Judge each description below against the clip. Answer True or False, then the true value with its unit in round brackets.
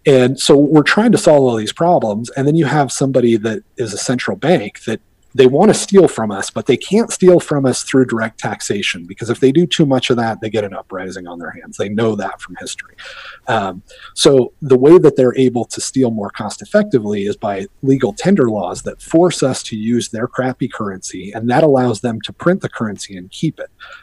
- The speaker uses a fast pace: True (225 wpm)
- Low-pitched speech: True (130 Hz)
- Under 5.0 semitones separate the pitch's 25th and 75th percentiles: False (5.3 semitones)